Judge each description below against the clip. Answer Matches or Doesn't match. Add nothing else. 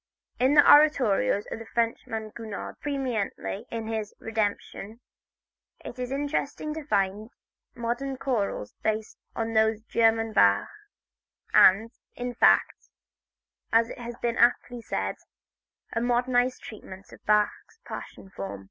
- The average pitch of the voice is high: Matches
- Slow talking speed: Matches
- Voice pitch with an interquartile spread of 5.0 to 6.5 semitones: Doesn't match